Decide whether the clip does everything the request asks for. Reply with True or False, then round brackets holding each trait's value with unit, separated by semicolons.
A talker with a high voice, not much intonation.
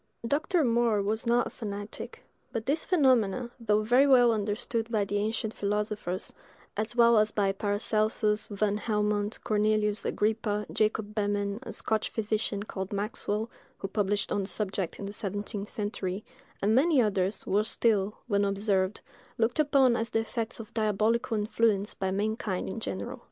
True (215 Hz; 2.0 semitones)